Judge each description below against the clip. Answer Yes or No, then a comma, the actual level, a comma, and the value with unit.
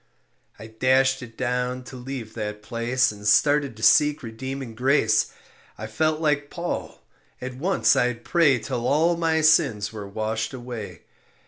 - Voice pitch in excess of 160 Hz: No, low, 125 Hz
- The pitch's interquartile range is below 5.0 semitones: Yes, average, 4.3 semitones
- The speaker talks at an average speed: Yes, average, 150 wpm